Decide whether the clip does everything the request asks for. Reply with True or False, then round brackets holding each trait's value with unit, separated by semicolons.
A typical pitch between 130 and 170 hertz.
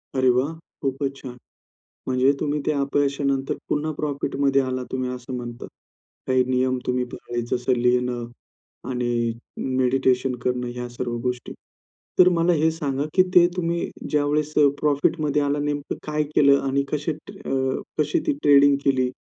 True (135 Hz)